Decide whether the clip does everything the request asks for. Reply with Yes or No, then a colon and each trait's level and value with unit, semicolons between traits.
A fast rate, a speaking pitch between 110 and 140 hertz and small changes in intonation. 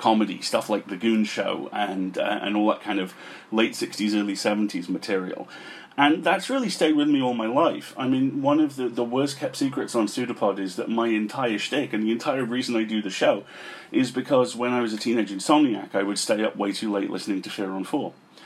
No: fast, 230 wpm; low, 115 Hz; average, 4.2 semitones